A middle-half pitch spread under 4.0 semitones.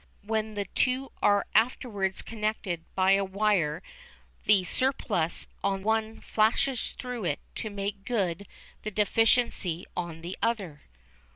Yes: average, 3.0 semitones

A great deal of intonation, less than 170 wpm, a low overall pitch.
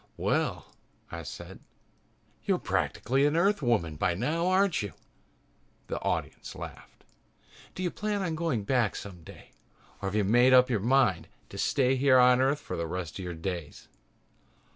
Yes: wide, 7.5 semitones; average, 160 wpm; low, 125 Hz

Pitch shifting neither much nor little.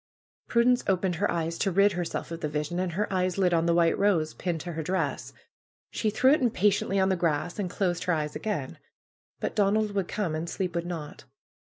Yes: average, 3.0 semitones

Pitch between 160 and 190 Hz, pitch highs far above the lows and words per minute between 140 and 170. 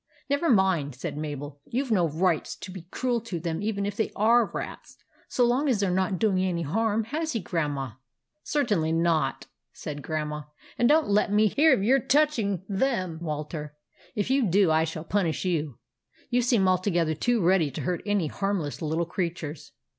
No: medium, 185 Hz; wide, 5.9 semitones; average, 200 wpm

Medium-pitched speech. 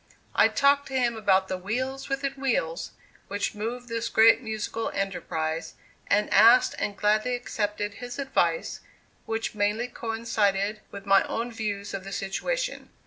No: high, 220 Hz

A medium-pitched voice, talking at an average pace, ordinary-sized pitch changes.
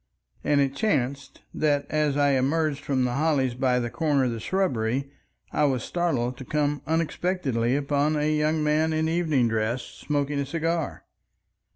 Yes: medium, 145 Hz; average, 165 wpm; average, 3.1 semitones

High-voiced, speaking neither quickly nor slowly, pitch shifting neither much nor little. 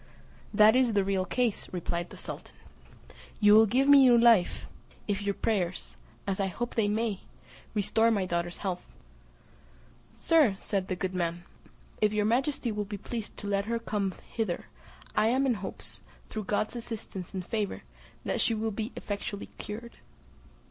Yes: high, 210 Hz; average, 165 wpm; average, 3.0 semitones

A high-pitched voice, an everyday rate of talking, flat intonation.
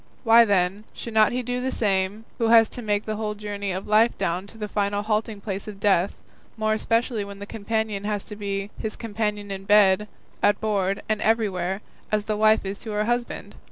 No: high, 210 Hz; fast, 210 wpm; narrow, 1.6 semitones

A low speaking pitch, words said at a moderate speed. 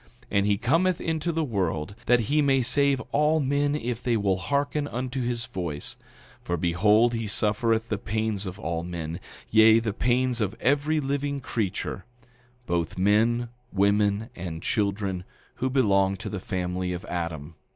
Yes: low, 110 Hz; average, 160 wpm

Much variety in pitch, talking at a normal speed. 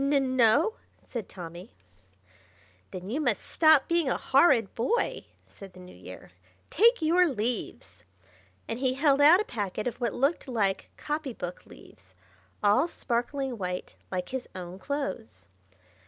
Yes: wide, 7.0 semitones; average, 145 wpm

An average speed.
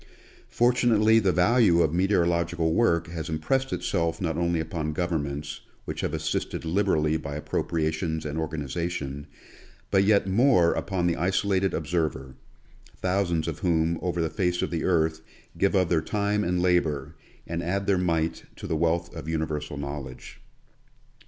Yes: average, 150 wpm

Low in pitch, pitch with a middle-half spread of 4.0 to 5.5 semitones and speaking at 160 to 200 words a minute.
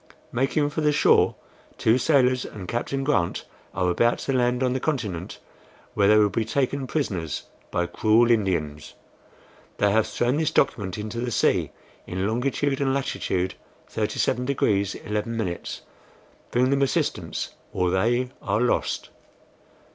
No: low, 120 Hz; average, 4.8 semitones; average, 140 wpm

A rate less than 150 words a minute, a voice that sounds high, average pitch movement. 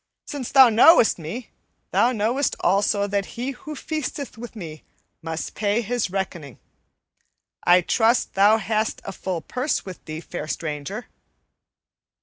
No: slow, 135 wpm; high, 210 Hz; wide, 5.7 semitones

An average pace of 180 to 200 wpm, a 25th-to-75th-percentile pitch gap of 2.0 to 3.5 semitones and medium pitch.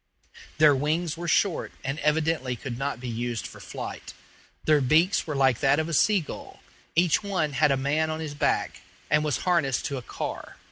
Yes: average, 195 wpm; average, 2.9 semitones; medium, 150 Hz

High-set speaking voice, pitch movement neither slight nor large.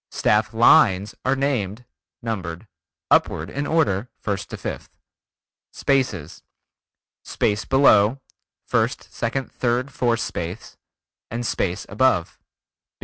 No: low, 115 Hz; average, 4.8 semitones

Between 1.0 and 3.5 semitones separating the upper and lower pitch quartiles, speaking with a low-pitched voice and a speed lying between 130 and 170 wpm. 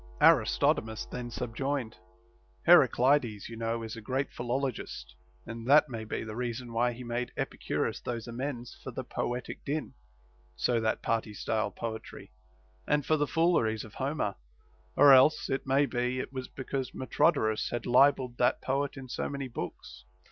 Yes: average, 2.9 semitones; low, 125 Hz; average, 160 wpm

